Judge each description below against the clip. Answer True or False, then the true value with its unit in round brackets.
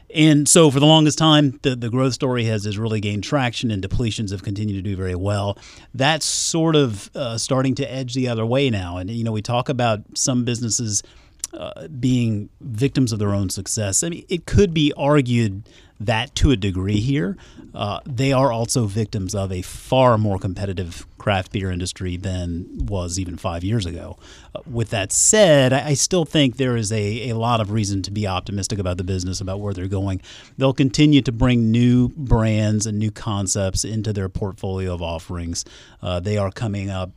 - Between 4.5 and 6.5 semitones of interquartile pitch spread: True (5.1 semitones)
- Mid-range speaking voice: False (110 Hz)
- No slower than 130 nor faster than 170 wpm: False (200 wpm)